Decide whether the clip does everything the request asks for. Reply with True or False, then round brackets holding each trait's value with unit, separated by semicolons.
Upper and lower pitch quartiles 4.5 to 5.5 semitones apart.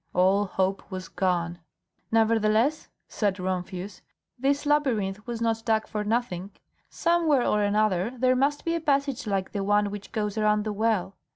False (3.8 semitones)